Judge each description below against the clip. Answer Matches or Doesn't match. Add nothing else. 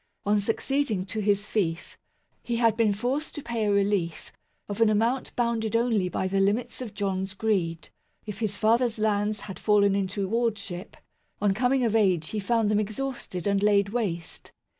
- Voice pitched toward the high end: Matches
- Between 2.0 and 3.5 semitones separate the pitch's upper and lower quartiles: Matches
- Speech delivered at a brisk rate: Doesn't match